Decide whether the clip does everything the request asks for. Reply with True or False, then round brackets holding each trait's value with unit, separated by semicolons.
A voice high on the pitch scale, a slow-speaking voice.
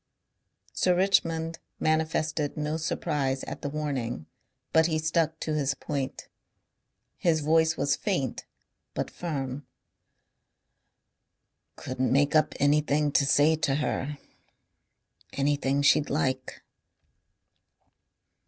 False (150 Hz; 100 wpm)